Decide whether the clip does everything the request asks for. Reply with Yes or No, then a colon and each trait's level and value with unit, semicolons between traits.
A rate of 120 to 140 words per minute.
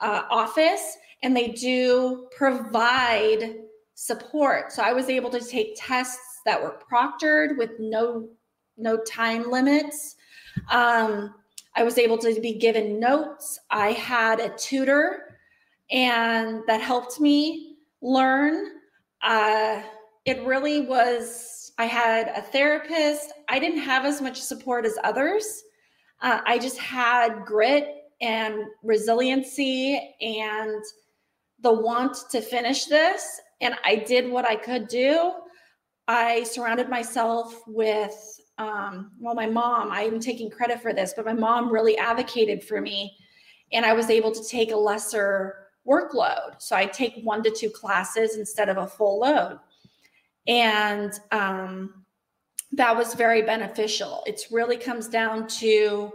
Yes: slow, 135 wpm